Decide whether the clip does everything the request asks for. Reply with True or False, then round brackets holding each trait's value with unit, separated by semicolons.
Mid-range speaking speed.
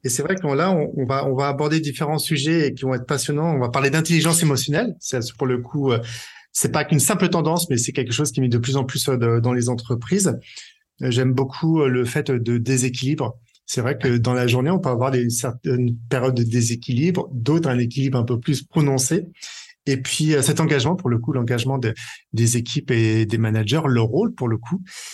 True (205 wpm)